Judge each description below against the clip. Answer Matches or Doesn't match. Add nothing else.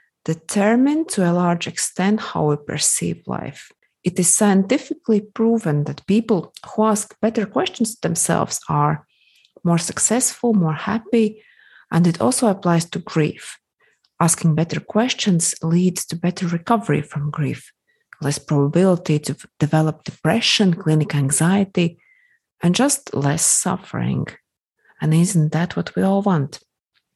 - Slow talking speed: Matches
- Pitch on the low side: Doesn't match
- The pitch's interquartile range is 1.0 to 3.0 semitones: Doesn't match